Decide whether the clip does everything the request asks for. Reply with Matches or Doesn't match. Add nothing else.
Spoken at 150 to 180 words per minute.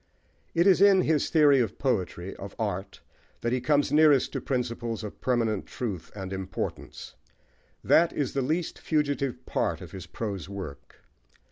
Matches